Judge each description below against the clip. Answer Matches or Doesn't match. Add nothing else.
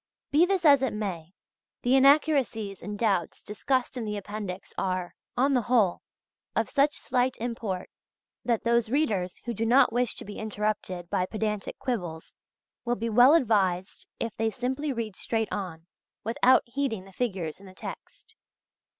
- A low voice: Doesn't match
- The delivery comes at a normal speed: Matches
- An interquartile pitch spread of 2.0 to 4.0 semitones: Doesn't match